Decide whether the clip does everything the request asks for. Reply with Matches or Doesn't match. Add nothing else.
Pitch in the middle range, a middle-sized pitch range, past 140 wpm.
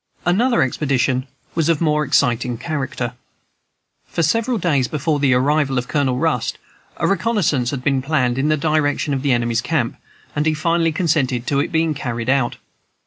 Matches